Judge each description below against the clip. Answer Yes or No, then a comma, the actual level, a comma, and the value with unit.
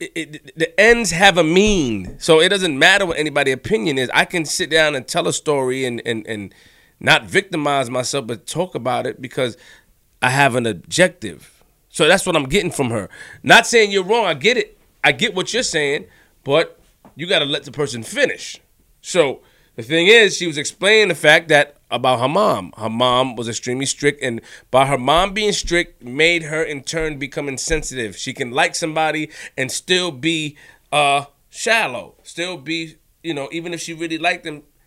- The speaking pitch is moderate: Yes, medium, 155 Hz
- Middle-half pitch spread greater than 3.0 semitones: Yes, average, 4.6 semitones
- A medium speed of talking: Yes, average, 195 wpm